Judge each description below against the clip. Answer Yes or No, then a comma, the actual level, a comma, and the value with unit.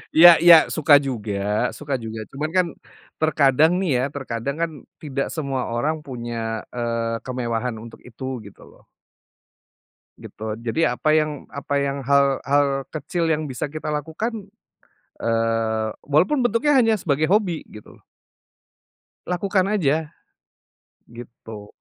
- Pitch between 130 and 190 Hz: Yes, medium, 140 Hz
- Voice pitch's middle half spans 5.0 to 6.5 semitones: Yes, average, 5.3 semitones